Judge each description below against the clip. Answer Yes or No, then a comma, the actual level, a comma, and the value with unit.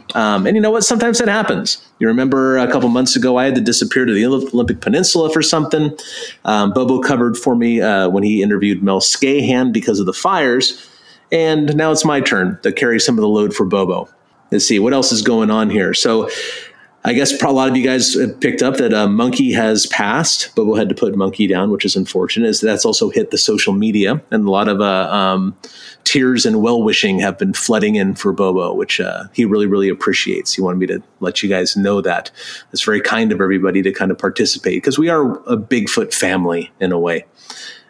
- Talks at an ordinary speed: No, fast, 220 wpm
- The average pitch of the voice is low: Yes, low, 120 Hz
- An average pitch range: No, wide, 7.9 semitones